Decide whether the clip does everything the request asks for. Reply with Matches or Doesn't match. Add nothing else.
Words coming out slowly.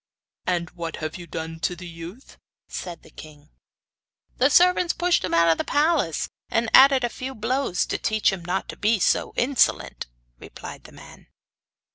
Doesn't match